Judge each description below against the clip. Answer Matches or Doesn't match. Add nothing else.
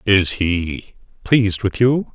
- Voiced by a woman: Doesn't match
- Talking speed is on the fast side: Doesn't match